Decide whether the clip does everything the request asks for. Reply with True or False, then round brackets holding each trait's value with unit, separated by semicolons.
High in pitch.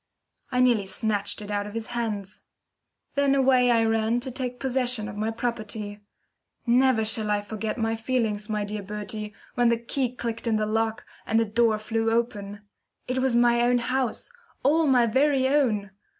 True (225 Hz)